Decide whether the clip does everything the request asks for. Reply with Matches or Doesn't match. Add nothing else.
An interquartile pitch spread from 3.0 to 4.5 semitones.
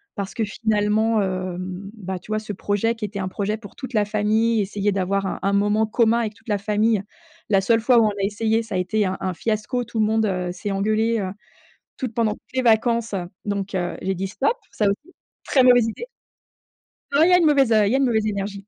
Doesn't match